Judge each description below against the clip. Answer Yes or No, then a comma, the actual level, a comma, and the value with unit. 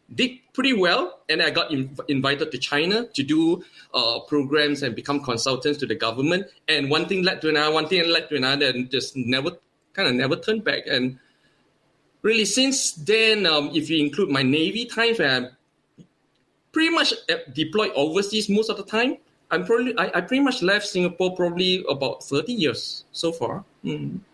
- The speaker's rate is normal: Yes, average, 180 wpm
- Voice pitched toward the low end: No, medium, 175 Hz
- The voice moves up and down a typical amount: No, wide, 7.1 semitones